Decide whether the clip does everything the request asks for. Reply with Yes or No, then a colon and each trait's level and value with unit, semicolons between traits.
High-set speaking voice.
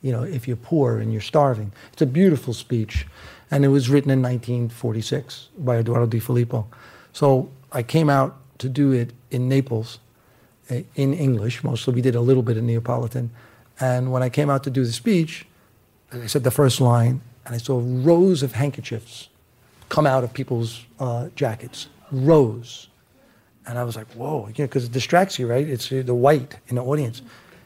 No: low, 125 Hz